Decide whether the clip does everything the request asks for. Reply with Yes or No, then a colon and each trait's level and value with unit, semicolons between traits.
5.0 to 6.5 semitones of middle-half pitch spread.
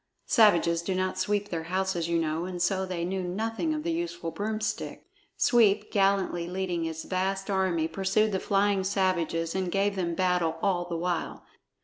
No: average, 2.7 semitones